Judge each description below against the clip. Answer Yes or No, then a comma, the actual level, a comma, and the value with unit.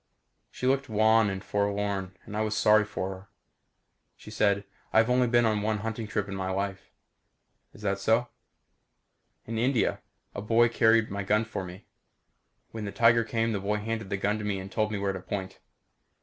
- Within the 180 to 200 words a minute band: Yes, average, 190 wpm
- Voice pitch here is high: No, low, 105 Hz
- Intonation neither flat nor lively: No, narrow, 2.2 semitones